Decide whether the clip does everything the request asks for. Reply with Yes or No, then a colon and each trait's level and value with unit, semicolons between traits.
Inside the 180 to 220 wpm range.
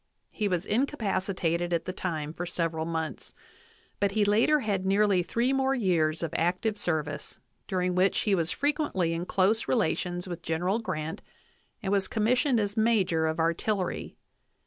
No: average, 160 wpm